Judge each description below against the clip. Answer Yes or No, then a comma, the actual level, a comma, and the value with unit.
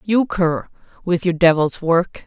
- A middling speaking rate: Yes, average, 160 wpm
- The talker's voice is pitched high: No, medium, 175 Hz